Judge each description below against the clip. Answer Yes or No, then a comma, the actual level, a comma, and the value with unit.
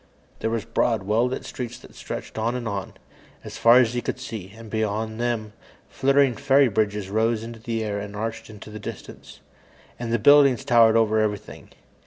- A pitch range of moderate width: No, narrow, 2.0 semitones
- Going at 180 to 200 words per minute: Yes, average, 190 wpm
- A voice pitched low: Yes, low, 115 Hz